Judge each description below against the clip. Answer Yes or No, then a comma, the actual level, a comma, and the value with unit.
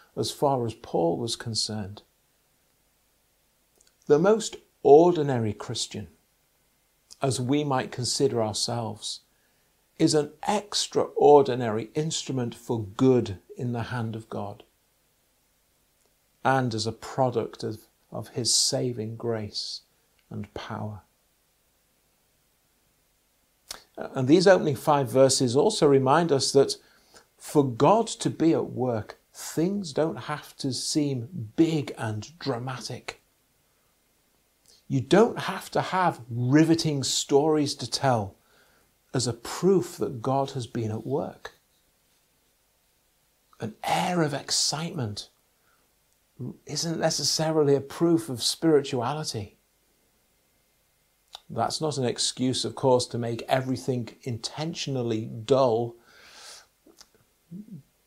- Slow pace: Yes, slow, 100 wpm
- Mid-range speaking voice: No, low, 130 Hz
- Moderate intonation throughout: Yes, average, 4.6 semitones